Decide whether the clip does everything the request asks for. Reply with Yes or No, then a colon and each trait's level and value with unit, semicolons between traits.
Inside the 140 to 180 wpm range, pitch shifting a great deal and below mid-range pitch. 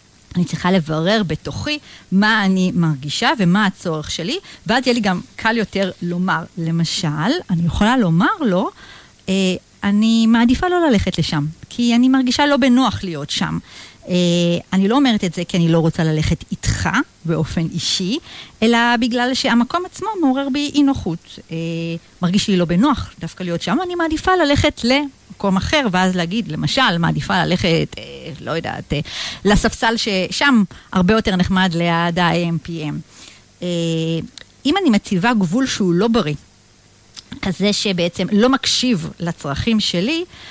No: fast, 150 wpm; wide, 6.0 semitones; medium, 185 Hz